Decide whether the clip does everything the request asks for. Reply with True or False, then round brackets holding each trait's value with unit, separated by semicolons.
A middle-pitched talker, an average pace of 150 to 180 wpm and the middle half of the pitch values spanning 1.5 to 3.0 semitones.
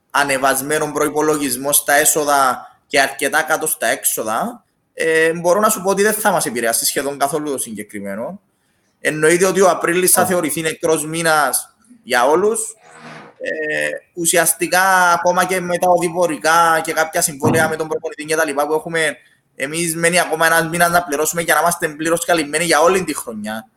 True (160 Hz; 170 wpm; 2.5 semitones)